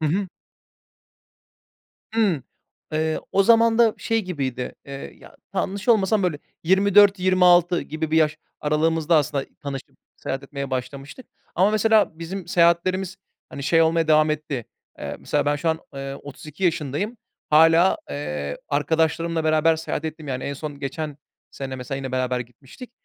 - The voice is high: No, medium, 160 Hz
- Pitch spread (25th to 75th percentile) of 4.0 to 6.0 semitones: Yes, average, 4.7 semitones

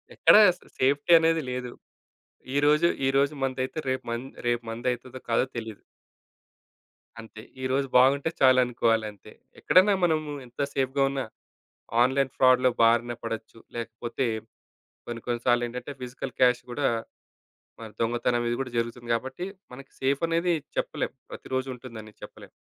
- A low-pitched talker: Yes, low, 125 Hz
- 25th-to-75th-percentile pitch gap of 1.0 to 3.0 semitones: Yes, narrow, 2.5 semitones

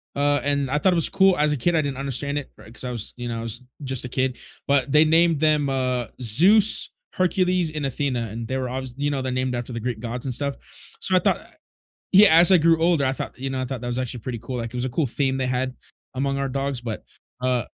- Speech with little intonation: No, average, 3.2 semitones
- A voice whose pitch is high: No, low, 135 Hz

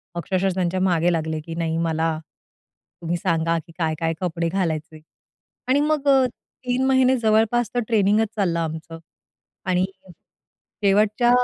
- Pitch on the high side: No, medium, 180 Hz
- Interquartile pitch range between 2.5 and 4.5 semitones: No, average, 5.2 semitones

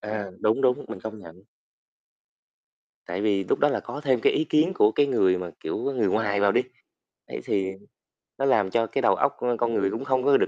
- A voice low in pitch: Yes, low, 110 Hz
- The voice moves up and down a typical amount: Yes, average, 4.7 semitones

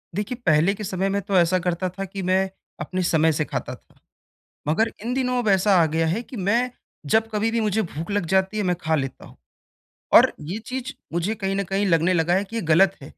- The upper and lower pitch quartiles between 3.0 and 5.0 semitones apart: Yes, average, 3.8 semitones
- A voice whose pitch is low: No, high, 195 Hz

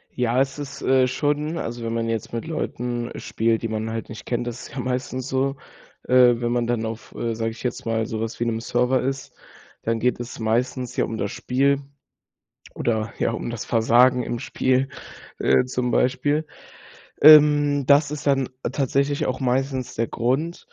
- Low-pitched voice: Yes, low, 125 Hz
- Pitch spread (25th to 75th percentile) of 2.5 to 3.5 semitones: Yes, average, 2.8 semitones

